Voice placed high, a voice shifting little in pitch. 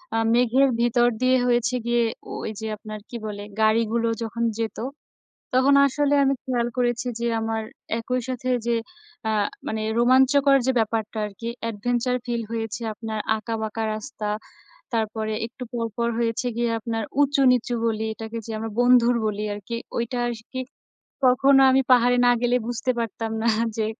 Yes: high, 235 Hz; narrow, 2.0 semitones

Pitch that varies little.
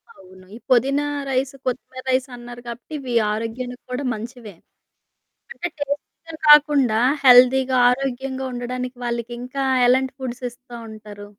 Yes: narrow, 1.8 semitones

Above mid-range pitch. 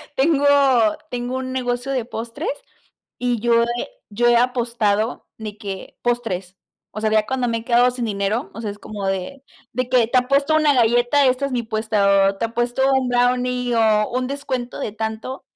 Yes: high, 240 Hz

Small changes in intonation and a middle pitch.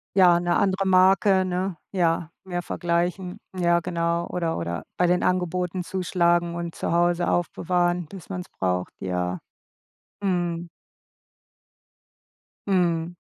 Yes: narrow, 1.3 semitones; medium, 175 Hz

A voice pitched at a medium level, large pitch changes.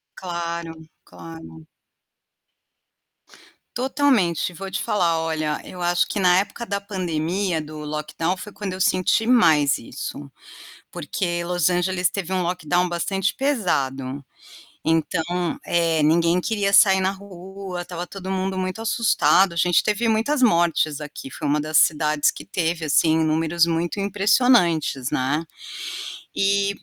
No: medium, 175 Hz; average, 3.6 semitones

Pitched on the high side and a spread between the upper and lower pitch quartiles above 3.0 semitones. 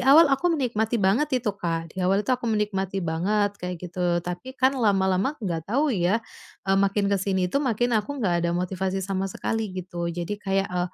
Yes: high, 195 Hz; average, 3.6 semitones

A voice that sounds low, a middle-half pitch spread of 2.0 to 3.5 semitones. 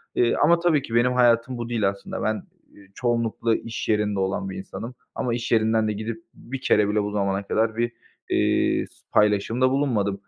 Yes: low, 115 Hz; average, 2.9 semitones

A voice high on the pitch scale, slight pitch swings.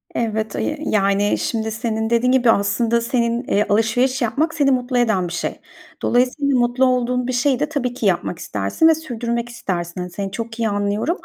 No: high, 235 Hz; average, 3.1 semitones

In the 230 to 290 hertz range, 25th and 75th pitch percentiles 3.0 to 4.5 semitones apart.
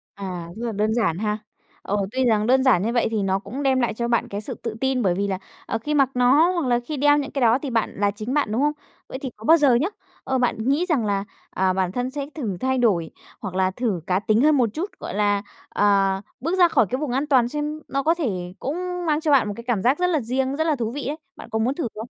No: high, 245 Hz; average, 5.2 semitones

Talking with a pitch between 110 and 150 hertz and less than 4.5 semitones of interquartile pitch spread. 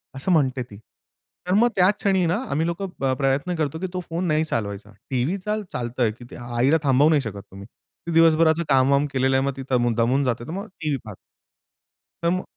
No: medium, 140 Hz; wide, 5.5 semitones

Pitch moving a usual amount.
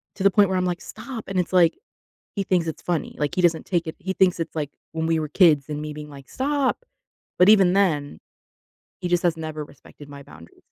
Yes: average, 3.8 semitones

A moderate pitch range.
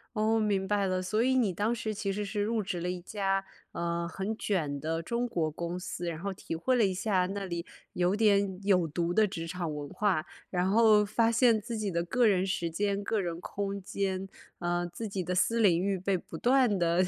Yes: average, 3.3 semitones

